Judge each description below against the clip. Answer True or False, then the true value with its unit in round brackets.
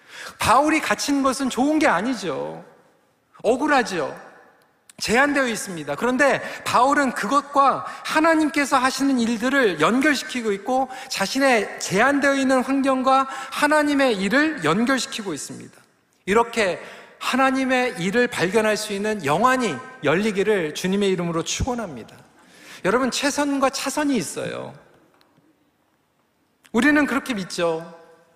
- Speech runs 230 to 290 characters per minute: True (280 characters per minute)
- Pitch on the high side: True (260 Hz)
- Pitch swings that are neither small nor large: True (4.3 semitones)